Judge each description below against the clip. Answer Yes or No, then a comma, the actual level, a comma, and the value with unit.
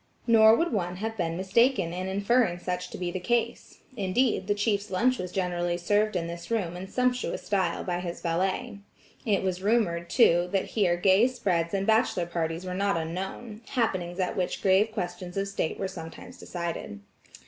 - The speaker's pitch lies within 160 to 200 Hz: Yes, high, 190 Hz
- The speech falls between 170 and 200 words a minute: Yes, average, 180 wpm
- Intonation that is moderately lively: Yes, average, 3.5 semitones